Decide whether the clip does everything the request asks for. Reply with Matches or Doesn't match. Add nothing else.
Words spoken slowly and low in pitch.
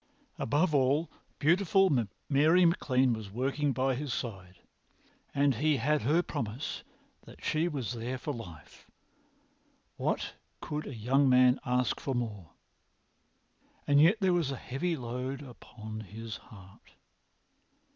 Matches